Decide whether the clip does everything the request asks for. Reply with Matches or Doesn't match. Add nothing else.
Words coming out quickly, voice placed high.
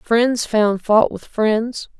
Doesn't match